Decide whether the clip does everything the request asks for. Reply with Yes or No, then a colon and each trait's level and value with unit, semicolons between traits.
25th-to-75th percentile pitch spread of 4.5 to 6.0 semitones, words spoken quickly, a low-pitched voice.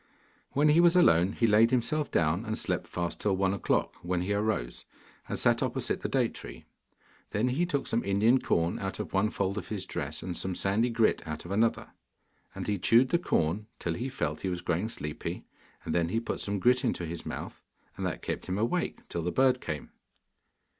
Yes: average, 5.2 semitones; fast, 210 wpm; low, 100 Hz